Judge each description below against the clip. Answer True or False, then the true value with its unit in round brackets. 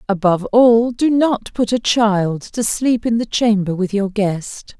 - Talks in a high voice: True (215 Hz)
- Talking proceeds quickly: False (190 wpm)